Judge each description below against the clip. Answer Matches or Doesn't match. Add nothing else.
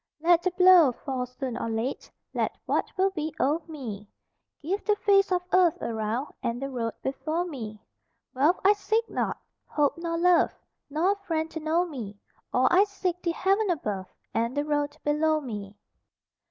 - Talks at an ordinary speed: Matches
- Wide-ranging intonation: Matches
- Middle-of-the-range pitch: Doesn't match